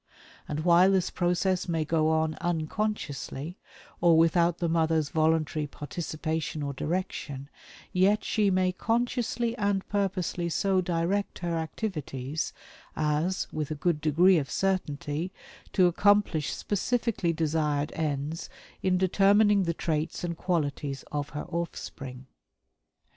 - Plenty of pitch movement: No, average, 3.5 semitones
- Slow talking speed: Yes, slow, 120 wpm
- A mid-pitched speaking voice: Yes, medium, 170 Hz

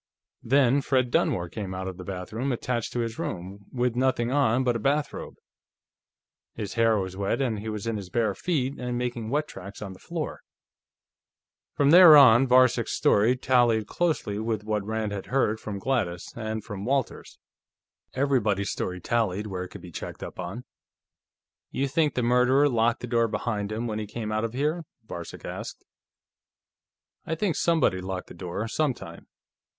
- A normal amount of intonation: Yes, average, 4.0 semitones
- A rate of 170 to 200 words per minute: Yes, average, 175 wpm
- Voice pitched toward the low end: Yes, low, 115 Hz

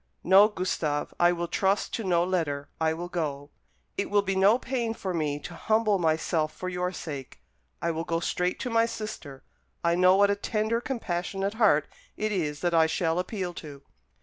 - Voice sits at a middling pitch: Yes, medium, 180 Hz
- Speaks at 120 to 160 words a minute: No, average, 190 wpm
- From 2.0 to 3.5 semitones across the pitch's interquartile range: No, average, 4.0 semitones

